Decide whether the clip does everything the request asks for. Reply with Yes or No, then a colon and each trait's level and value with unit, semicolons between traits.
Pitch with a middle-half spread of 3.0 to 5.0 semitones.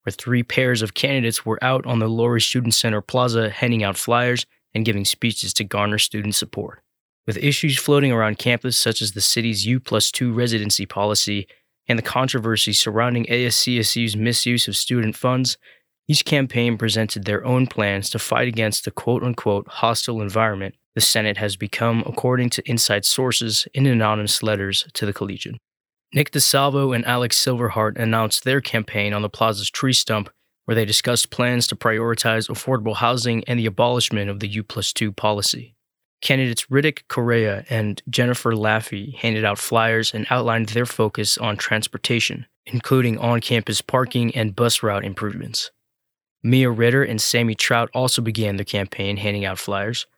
No: narrow, 2.6 semitones